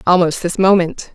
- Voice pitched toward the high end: No, medium, 180 Hz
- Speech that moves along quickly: No, average, 155 wpm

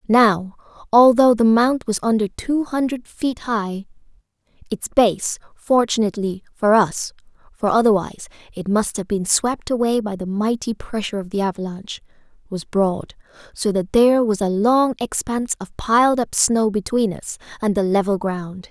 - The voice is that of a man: No, female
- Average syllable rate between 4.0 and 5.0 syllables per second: Yes, 4.7 syllables/s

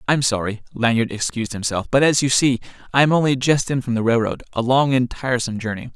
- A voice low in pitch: Yes, low, 125 Hz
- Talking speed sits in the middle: No, fast, 220 wpm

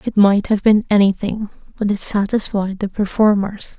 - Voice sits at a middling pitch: No, high, 205 Hz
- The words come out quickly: No, average, 160 wpm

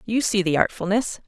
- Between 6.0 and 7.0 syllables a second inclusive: No, 5.3 syllables/s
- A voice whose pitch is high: Yes, high, 200 Hz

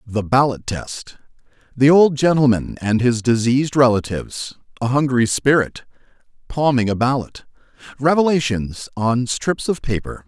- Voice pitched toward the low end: Yes, low, 130 Hz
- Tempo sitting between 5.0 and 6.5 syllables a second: No, 4.6 syllables/s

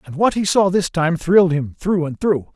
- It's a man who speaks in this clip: Yes, male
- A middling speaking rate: No, fast, 260 wpm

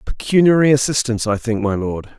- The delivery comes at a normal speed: Yes, average, 165 wpm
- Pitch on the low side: Yes, low, 125 Hz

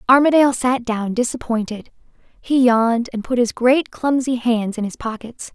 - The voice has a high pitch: Yes, high, 240 Hz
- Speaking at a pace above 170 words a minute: No, average, 160 wpm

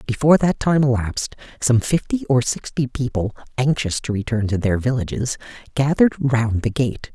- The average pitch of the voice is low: Yes, low, 125 Hz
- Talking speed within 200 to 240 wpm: No, average, 160 wpm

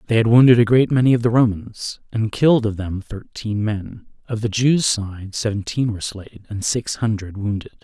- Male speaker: Yes, male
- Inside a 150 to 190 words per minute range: No, average, 200 wpm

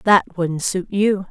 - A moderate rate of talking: Yes, average, 185 wpm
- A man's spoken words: No, female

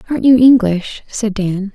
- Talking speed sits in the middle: Yes, average, 170 wpm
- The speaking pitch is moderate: No, high, 215 Hz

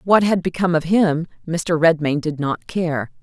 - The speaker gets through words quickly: No, average, 185 wpm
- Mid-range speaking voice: Yes, medium, 165 Hz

